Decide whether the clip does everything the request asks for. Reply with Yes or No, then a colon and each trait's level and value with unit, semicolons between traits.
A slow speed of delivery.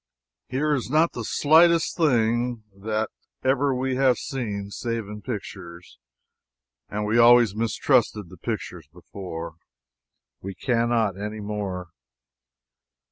Yes: slow, 110 wpm